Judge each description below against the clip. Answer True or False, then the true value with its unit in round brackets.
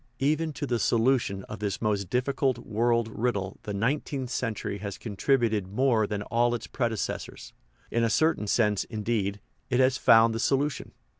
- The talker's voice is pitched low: True (115 Hz)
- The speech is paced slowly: False (160 wpm)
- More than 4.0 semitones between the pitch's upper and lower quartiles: False (3.6 semitones)